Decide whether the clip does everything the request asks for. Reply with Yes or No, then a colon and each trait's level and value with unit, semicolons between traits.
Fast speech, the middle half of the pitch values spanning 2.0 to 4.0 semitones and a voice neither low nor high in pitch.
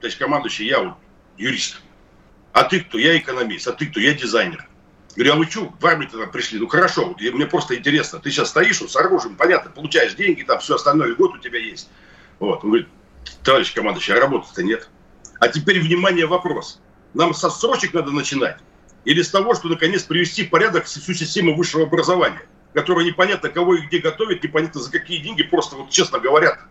Yes: fast, 200 wpm; average, 3.3 semitones; medium, 175 Hz